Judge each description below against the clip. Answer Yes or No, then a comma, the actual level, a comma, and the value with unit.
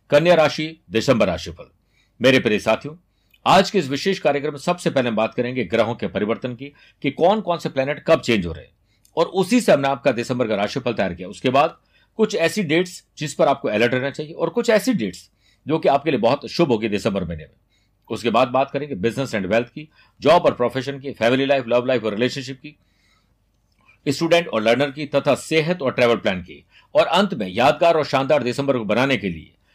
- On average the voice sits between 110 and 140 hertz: Yes, low, 135 Hz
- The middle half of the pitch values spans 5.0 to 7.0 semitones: Yes, average, 5.3 semitones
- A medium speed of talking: No, fast, 215 wpm